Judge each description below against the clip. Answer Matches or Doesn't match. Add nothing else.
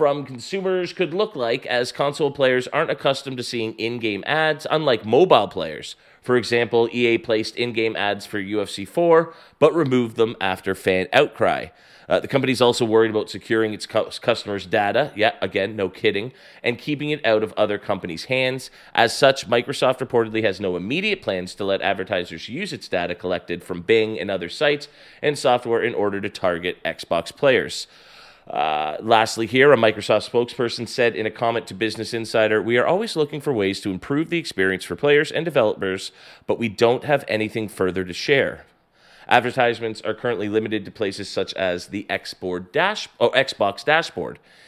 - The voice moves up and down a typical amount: Matches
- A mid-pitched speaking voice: Doesn't match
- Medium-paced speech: Matches